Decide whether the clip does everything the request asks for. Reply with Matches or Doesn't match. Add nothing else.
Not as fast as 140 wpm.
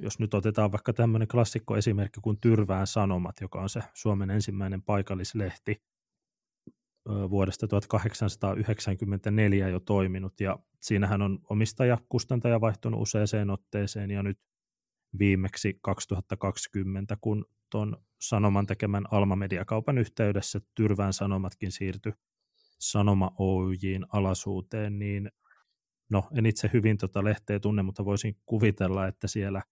Matches